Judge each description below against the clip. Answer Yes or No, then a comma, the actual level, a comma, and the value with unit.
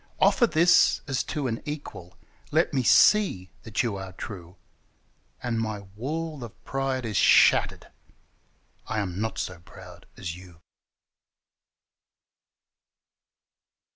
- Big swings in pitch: Yes, wide, 6.5 semitones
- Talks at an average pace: No, slow, 120 wpm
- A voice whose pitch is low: Yes, low, 115 Hz